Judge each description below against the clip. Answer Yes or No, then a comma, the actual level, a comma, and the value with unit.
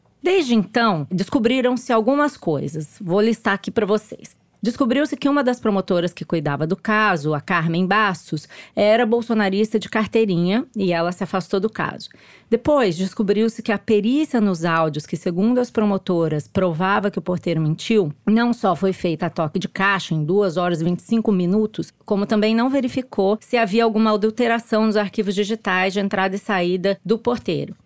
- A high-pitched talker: Yes, high, 205 Hz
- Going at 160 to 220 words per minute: Yes, average, 170 wpm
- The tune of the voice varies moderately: Yes, average, 3.8 semitones